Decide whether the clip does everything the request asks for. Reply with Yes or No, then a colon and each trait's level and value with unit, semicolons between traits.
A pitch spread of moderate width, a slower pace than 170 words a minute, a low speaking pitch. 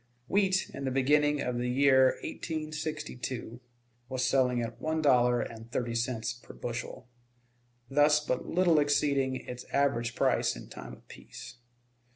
Yes: average, 3.4 semitones; average, 145 wpm; low, 130 Hz